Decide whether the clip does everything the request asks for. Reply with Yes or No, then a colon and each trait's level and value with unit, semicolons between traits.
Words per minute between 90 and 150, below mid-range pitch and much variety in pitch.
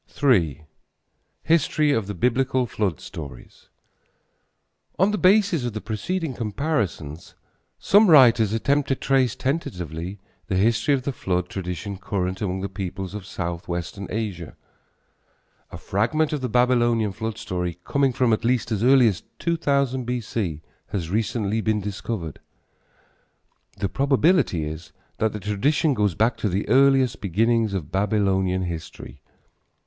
Yes: slow, 135 wpm; low, 110 Hz; wide, 5.7 semitones